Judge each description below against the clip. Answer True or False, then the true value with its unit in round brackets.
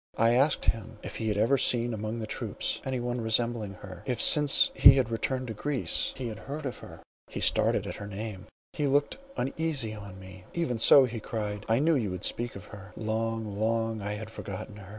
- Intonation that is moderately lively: True (3.5 semitones)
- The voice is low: True (115 Hz)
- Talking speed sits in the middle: False (210 wpm)